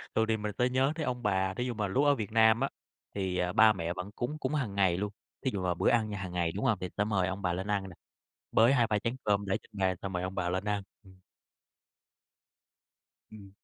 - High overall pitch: No, low, 100 Hz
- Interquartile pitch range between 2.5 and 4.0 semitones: Yes, average, 3.3 semitones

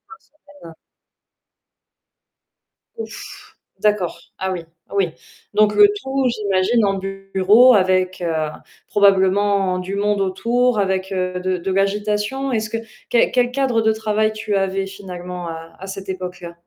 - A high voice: Yes, high, 195 Hz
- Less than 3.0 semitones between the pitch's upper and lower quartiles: Yes, narrow, 2.6 semitones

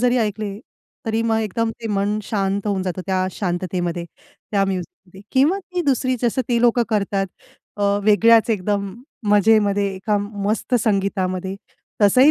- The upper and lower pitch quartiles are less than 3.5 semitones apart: Yes, average, 2.7 semitones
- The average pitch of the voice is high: Yes, high, 205 Hz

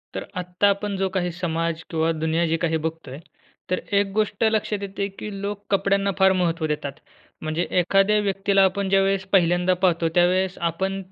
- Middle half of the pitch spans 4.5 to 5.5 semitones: No, average, 2.9 semitones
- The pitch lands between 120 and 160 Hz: No, medium, 185 Hz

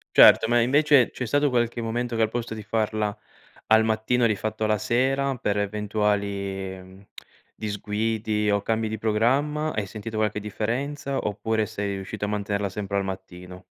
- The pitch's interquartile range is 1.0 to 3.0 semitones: Yes, narrow, 2.4 semitones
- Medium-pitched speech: No, low, 110 Hz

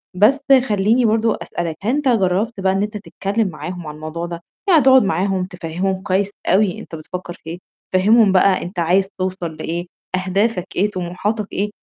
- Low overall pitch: No, high, 190 Hz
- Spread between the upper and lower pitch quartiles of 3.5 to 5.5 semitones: No, average, 3.1 semitones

